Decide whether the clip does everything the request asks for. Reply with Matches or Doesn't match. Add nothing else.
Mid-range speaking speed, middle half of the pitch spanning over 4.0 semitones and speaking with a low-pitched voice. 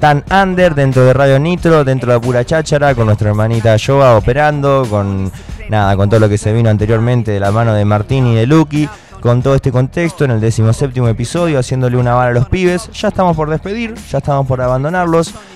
Doesn't match